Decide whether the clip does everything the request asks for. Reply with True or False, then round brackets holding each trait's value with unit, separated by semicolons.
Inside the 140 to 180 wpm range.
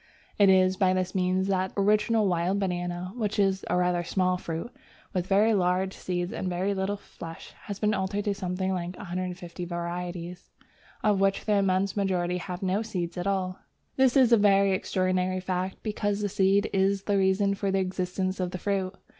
False (190 wpm)